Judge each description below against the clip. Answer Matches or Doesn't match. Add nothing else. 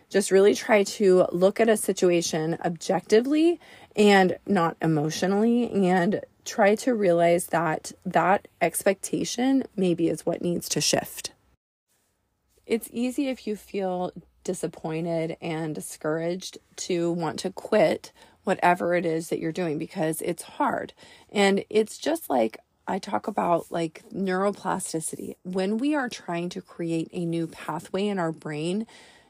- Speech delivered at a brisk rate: Doesn't match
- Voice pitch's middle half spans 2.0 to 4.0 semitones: Matches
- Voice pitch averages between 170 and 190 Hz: Matches